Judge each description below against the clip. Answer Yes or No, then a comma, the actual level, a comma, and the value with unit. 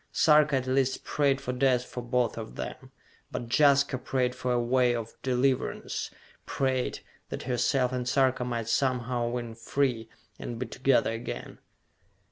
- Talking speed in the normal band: Yes, average, 150 wpm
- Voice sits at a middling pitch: No, low, 125 Hz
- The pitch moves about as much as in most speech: No, narrow, 1.7 semitones